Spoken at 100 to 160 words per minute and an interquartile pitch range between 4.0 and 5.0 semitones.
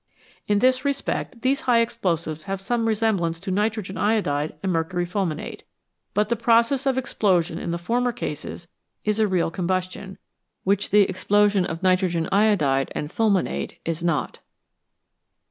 Yes: average, 145 wpm; average, 4.7 semitones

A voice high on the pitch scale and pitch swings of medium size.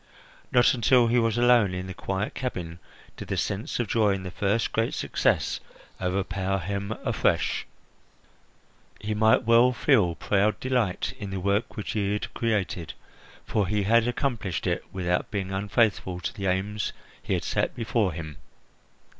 No: low, 100 Hz; average, 3.3 semitones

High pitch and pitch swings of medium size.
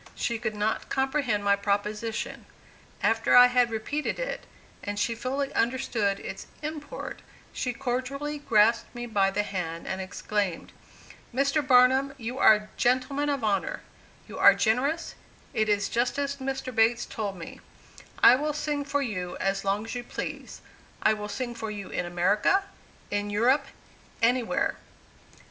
Yes: high, 235 Hz; average, 4.6 semitones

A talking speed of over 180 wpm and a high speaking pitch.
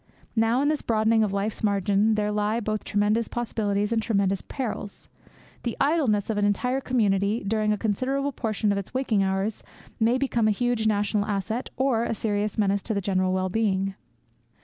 No: average, 175 wpm; high, 215 Hz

